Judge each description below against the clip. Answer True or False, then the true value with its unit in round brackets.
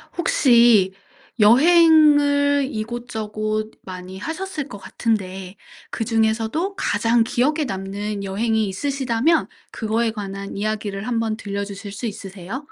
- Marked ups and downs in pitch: False (4.7 semitones)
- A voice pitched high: True (220 Hz)